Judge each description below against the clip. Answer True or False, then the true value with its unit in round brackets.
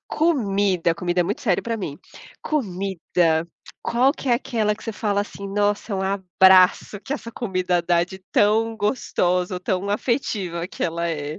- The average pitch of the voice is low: False (195 Hz)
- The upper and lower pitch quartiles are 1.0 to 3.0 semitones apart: False (3.7 semitones)